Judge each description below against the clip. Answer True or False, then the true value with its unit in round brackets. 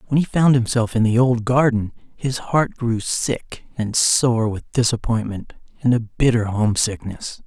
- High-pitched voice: False (115 Hz)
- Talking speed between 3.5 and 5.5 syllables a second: True (4.3 syllables/s)